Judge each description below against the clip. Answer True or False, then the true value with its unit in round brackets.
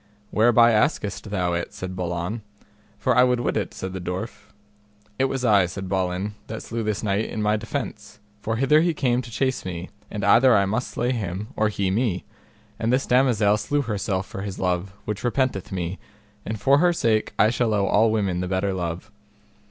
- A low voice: True (105 Hz)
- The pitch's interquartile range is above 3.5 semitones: True (4.2 semitones)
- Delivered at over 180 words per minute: True (200 wpm)